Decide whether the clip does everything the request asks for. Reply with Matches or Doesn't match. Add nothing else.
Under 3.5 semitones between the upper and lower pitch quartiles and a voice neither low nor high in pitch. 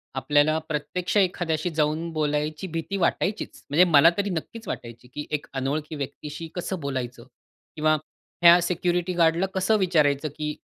Matches